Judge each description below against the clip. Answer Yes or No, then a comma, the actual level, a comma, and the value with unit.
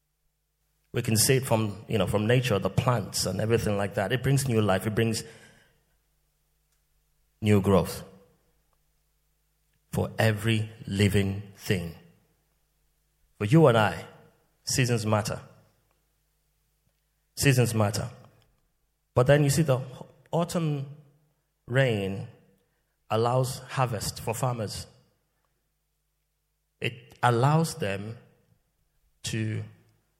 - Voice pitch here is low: Yes, low, 120 Hz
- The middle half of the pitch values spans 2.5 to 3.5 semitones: No, average, 5.0 semitones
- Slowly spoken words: Yes, slow, 100 wpm